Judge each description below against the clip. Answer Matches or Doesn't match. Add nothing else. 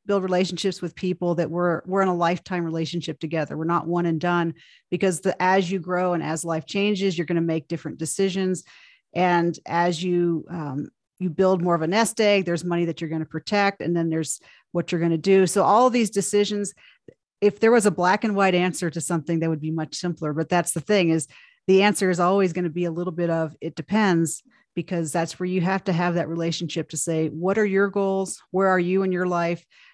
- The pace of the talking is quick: Matches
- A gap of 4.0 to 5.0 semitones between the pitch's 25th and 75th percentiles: Doesn't match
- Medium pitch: Matches